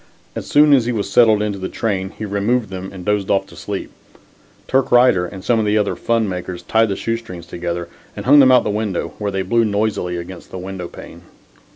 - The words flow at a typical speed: No, fast, 235 wpm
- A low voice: Yes, low, 100 Hz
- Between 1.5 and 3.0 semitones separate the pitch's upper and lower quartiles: No, average, 3.5 semitones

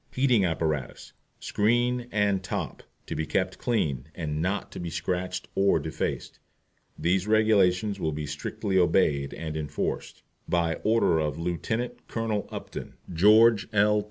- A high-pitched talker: No, very low, 95 Hz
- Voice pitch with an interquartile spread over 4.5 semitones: Yes, average, 5.2 semitones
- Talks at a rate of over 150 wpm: No, slow, 135 wpm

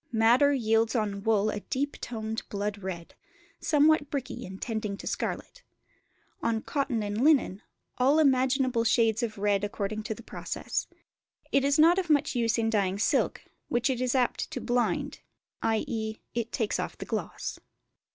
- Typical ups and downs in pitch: Yes, average, 3.7 semitones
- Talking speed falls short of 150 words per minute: No, average, 160 wpm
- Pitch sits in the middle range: No, high, 230 Hz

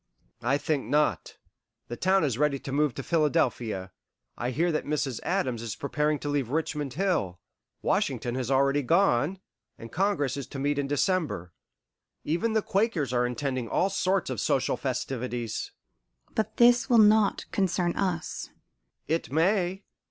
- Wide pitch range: Yes, wide, 6.2 semitones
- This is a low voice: No, medium, 145 Hz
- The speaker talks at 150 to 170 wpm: Yes, average, 155 wpm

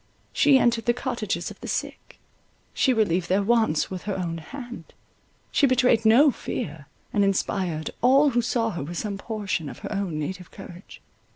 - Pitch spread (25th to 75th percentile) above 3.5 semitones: Yes, wide, 5.5 semitones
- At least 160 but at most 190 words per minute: Yes, average, 175 wpm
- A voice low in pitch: No, high, 205 Hz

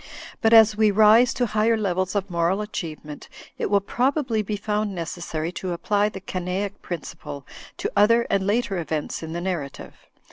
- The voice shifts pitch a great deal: No, average, 3.7 semitones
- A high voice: Yes, high, 200 Hz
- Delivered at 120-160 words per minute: No, average, 170 wpm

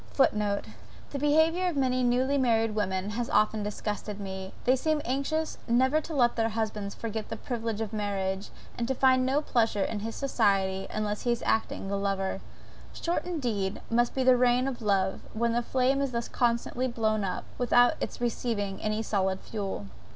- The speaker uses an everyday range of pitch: Yes, average, 3.8 semitones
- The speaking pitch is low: No, high, 230 Hz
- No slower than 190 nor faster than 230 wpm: No, average, 180 wpm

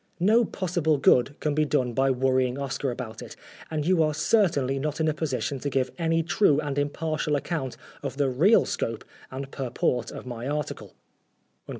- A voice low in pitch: No, medium, 145 Hz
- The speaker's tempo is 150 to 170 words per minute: No, average, 180 wpm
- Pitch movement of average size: Yes, average, 3.1 semitones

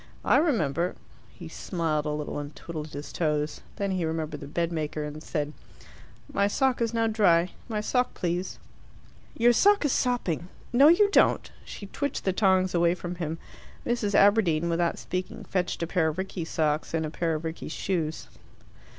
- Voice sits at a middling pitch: Yes, medium, 175 Hz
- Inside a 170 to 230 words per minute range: Yes, average, 175 wpm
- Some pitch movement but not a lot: Yes, average, 4.5 semitones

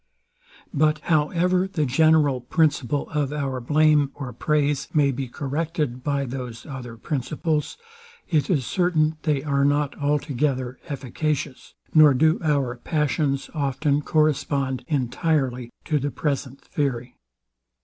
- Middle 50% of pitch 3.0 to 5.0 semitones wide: No, narrow, 2.6 semitones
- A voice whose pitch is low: No, medium, 145 Hz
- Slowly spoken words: Yes, slow, 120 wpm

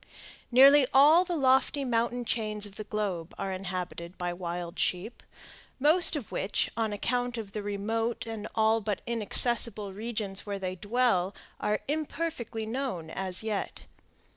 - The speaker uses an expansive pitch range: No, average, 4.1 semitones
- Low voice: No, high, 220 Hz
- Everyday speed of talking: Yes, average, 145 wpm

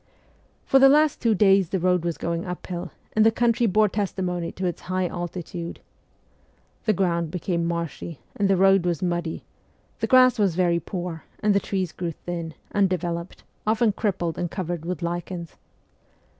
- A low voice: No, medium, 180 Hz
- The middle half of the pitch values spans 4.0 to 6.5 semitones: No, average, 2.7 semitones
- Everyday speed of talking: Yes, average, 170 wpm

